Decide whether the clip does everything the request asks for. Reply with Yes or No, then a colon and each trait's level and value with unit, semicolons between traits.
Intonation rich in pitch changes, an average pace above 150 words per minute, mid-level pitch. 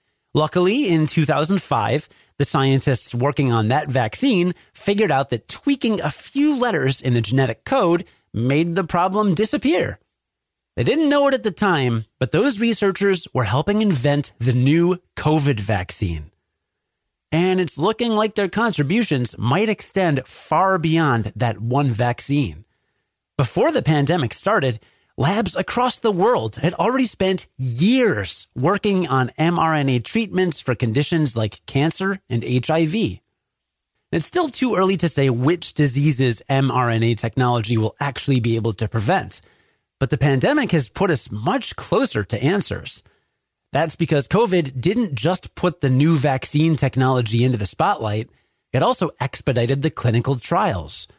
No: wide, 7.0 semitones; average, 140 wpm; medium, 145 Hz